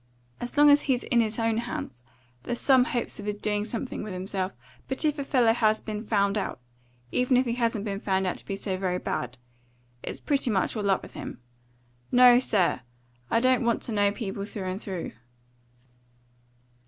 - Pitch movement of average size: Yes, average, 3.8 semitones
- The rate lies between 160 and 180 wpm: No, average, 195 wpm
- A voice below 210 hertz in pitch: No, high, 215 Hz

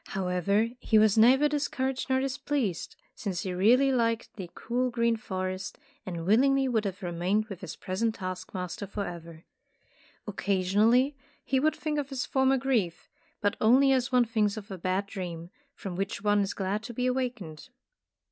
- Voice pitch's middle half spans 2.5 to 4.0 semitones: No, average, 5.2 semitones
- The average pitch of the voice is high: Yes, high, 215 Hz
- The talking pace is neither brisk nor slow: Yes, average, 170 wpm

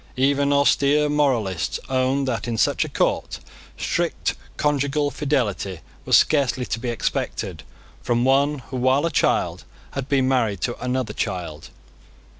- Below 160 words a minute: Yes, average, 140 wpm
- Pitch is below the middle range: Yes, low, 130 Hz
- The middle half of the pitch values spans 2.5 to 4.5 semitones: Yes, average, 3.1 semitones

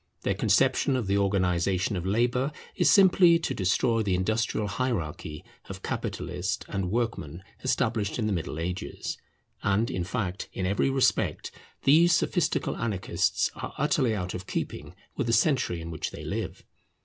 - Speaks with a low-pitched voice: Yes, low, 105 Hz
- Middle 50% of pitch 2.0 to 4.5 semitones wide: No, wide, 5.5 semitones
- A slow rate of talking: No, average, 155 wpm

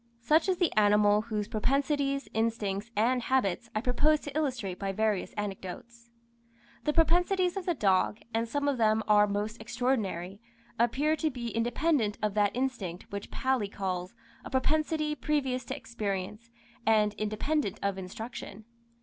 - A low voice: No, high, 230 Hz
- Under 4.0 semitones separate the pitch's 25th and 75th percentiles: No, average, 5.0 semitones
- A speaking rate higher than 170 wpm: No, average, 150 wpm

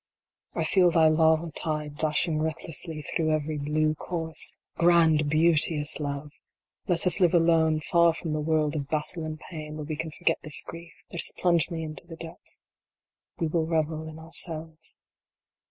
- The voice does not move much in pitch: Yes, narrow, 1.3 semitones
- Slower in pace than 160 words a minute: No, average, 170 wpm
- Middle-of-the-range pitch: Yes, medium, 160 Hz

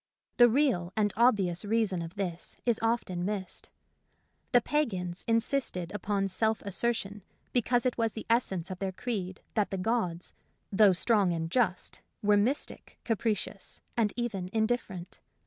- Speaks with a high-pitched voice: Yes, high, 210 Hz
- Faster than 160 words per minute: No, average, 145 wpm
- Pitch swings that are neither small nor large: Yes, average, 4.1 semitones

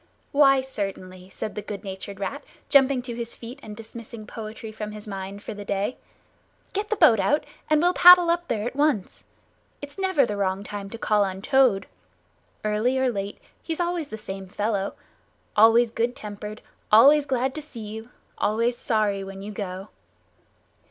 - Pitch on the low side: No, high, 220 Hz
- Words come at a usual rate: Yes, average, 175 wpm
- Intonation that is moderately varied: Yes, average, 4.8 semitones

